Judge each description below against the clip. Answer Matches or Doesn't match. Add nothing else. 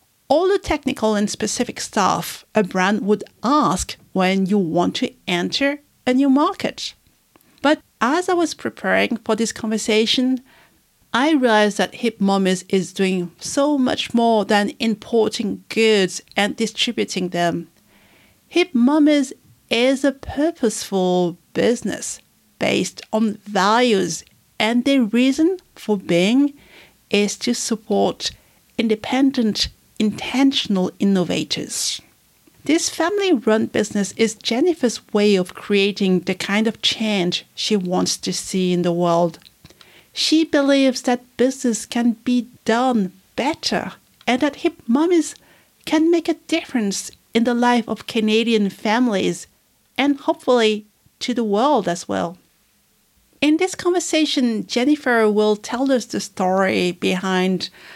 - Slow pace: Matches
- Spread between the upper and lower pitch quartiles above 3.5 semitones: Matches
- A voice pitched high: Matches